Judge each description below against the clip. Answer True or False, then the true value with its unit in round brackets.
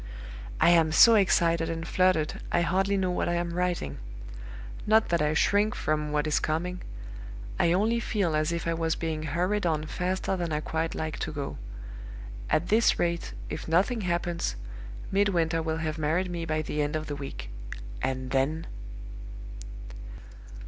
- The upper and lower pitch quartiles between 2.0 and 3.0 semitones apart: True (2.6 semitones)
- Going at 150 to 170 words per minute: True (165 wpm)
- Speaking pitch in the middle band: True (165 Hz)